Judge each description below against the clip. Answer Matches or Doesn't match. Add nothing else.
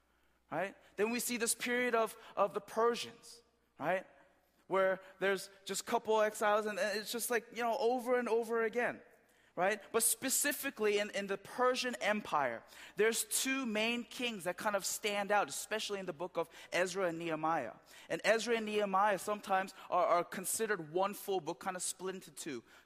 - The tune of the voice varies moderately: Matches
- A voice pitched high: Matches